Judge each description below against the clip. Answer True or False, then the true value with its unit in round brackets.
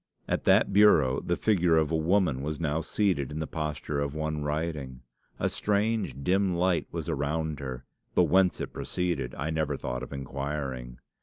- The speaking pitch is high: False (75 Hz)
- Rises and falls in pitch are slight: False (3.8 semitones)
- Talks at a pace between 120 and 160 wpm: False (175 wpm)